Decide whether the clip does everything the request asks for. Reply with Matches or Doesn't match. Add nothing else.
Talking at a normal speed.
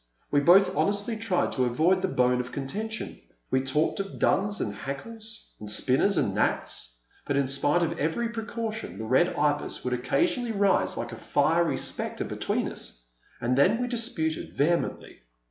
Matches